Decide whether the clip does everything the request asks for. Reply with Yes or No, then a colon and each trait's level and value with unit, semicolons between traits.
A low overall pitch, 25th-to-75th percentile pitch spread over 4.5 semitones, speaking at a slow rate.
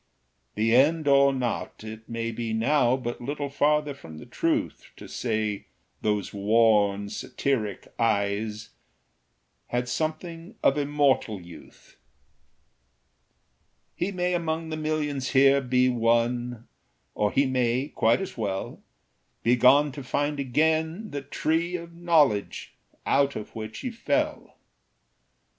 Yes: low, 130 Hz; average, 5.2 semitones; slow, 125 wpm